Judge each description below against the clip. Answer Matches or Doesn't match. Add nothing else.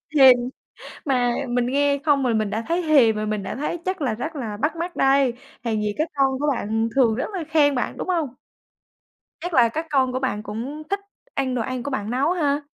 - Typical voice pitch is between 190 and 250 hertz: Doesn't match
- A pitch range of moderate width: Matches